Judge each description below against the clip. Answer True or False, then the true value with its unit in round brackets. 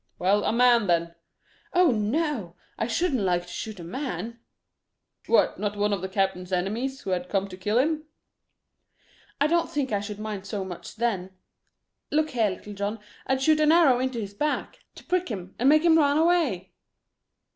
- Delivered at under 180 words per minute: False (185 wpm)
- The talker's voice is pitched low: False (220 Hz)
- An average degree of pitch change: False (6.9 semitones)